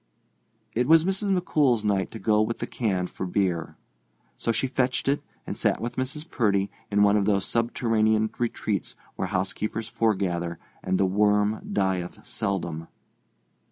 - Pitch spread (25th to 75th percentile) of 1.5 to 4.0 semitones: Yes, average, 3.6 semitones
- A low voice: Yes, low, 105 Hz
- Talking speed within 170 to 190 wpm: No, average, 160 wpm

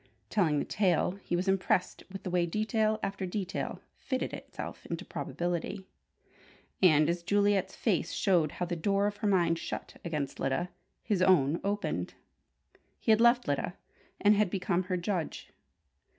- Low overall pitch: No, medium, 185 Hz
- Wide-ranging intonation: No, average, 3.0 semitones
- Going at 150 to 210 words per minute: Yes, average, 155 wpm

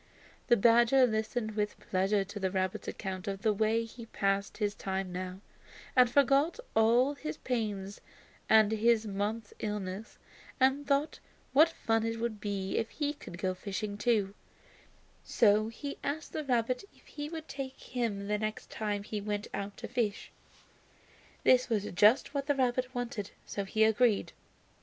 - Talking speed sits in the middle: Yes, average, 160 wpm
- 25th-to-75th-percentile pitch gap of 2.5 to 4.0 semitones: Yes, average, 3.7 semitones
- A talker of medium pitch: No, high, 220 Hz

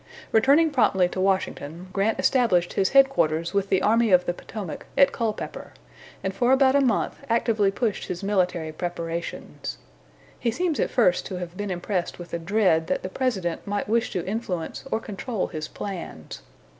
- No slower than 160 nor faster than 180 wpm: Yes, average, 170 wpm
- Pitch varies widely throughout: No, average, 4.6 semitones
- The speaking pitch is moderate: No, high, 195 Hz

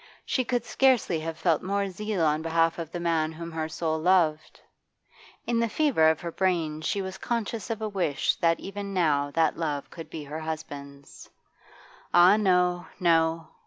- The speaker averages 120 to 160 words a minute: No, average, 175 wpm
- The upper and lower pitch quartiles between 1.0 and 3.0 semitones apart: No, average, 3.8 semitones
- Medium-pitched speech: Yes, medium, 170 Hz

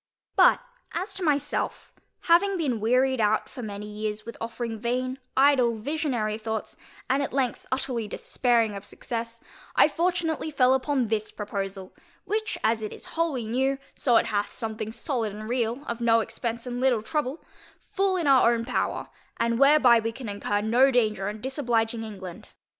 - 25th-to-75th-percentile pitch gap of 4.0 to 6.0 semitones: No, average, 3.6 semitones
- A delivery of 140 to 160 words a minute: No, average, 170 wpm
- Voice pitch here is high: Yes, high, 235 Hz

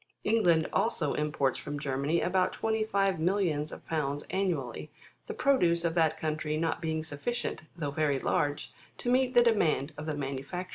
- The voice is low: No, medium, 160 Hz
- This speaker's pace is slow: No, average, 175 wpm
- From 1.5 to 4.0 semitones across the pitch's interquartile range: No, average, 4.5 semitones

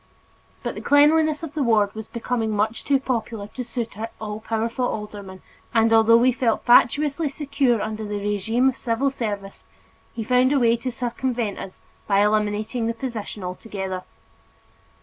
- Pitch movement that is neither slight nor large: Yes, average, 3.4 semitones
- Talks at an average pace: Yes, average, 165 wpm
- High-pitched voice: Yes, high, 230 Hz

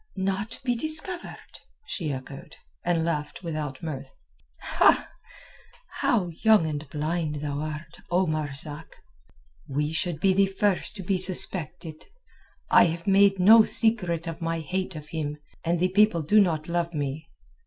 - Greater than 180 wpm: No, average, 145 wpm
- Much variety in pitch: No, average, 4.1 semitones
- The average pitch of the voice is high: No, medium, 170 Hz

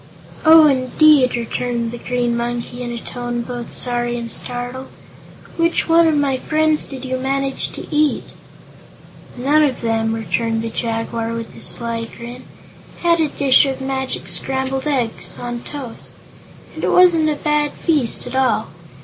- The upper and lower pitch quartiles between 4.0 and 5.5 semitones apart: No, average, 3.4 semitones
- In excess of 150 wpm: Yes, average, 160 wpm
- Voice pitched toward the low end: No, very high, 255 Hz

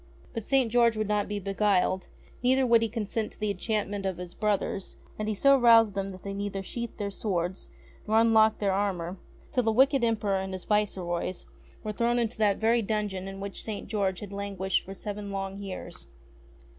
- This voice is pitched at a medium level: No, high, 205 Hz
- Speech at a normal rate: Yes, average, 195 wpm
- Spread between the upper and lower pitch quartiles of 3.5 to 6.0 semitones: No, narrow, 2.5 semitones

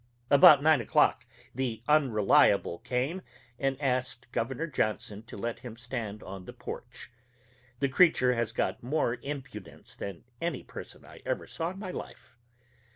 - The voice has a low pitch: Yes, low, 125 Hz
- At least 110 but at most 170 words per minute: Yes, average, 150 wpm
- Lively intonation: No, average, 4.1 semitones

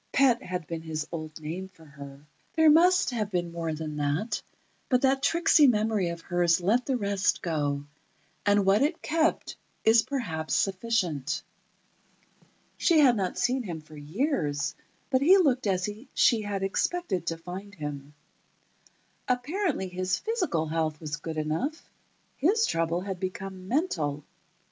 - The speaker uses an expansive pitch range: Yes, wide, 7.8 semitones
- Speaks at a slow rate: No, average, 150 wpm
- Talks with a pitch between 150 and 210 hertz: Yes, high, 190 Hz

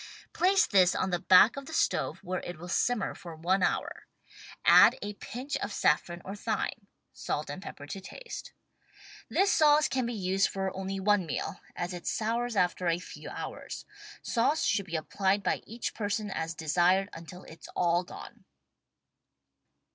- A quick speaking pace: No, average, 185 wpm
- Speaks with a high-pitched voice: Yes, high, 195 Hz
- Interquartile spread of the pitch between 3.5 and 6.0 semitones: Yes, average, 4.2 semitones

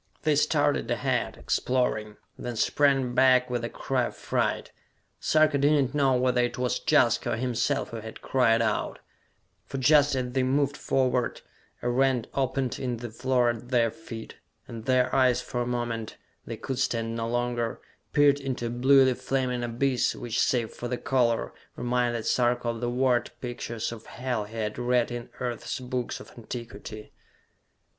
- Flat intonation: Yes, narrow, 1.8 semitones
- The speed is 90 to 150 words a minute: No, average, 170 wpm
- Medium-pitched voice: No, low, 125 Hz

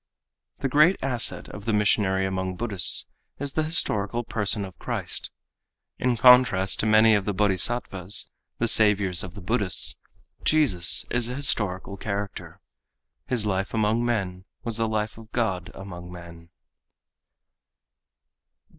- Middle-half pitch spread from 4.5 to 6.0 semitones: No, average, 3.7 semitones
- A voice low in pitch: Yes, low, 105 Hz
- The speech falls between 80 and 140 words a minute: Yes, slow, 135 wpm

